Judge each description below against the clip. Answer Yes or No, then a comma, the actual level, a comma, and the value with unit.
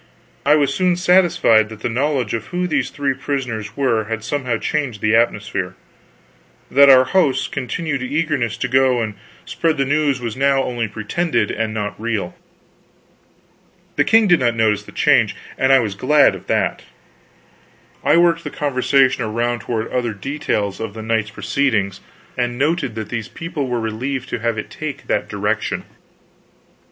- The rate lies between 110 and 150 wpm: No, average, 165 wpm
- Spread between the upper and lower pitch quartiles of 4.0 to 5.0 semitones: Yes, average, 4.3 semitones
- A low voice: Yes, low, 125 Hz